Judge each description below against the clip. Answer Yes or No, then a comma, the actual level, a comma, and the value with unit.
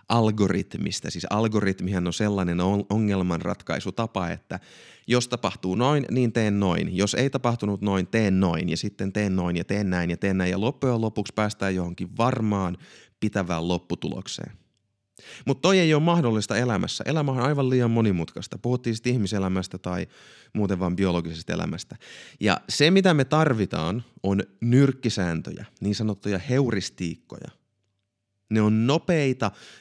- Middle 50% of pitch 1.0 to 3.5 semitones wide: No, average, 4.0 semitones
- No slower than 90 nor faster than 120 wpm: No, average, 140 wpm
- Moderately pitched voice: No, low, 105 Hz